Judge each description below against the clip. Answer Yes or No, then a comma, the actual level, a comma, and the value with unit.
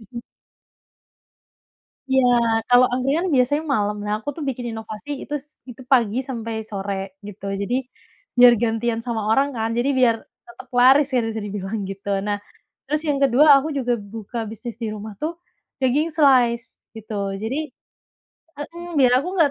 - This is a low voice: No, high, 245 Hz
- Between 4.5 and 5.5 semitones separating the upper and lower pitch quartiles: No, average, 3.5 semitones